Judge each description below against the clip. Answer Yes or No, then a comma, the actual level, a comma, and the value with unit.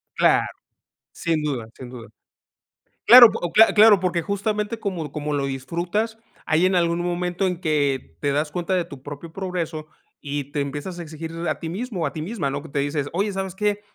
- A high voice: No, medium, 170 Hz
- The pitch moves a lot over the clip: No, average, 4.7 semitones